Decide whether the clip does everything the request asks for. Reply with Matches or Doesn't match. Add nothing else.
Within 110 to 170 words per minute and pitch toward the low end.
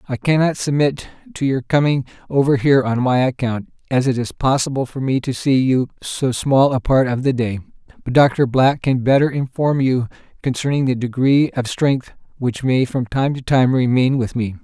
Doesn't match